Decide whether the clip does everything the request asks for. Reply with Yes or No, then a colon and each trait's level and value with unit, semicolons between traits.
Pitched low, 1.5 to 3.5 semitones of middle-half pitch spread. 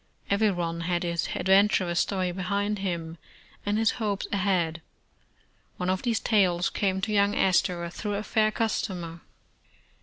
No: high, 190 Hz; average, 2.9 semitones